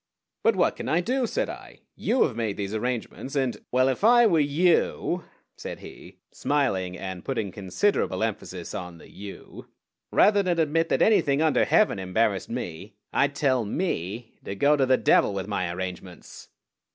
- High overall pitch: No, low, 125 Hz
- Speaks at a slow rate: No, average, 175 wpm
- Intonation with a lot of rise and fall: Yes, wide, 8.5 semitones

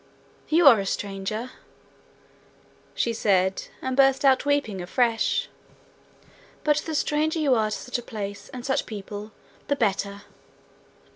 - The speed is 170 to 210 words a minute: No, slow, 135 wpm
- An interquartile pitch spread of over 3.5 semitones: Yes, average, 5.3 semitones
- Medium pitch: No, high, 235 Hz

